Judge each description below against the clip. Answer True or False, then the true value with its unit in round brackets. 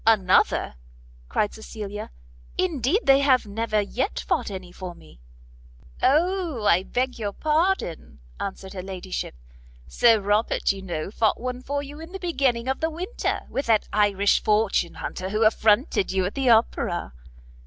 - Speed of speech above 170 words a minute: False (155 wpm)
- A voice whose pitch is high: True (220 Hz)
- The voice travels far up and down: True (5.9 semitones)